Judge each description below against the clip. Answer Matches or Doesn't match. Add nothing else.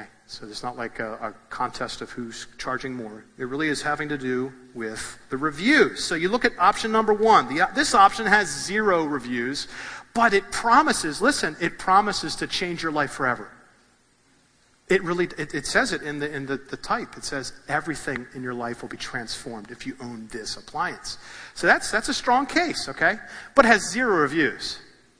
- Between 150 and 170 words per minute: Doesn't match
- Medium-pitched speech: Matches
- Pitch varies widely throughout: Matches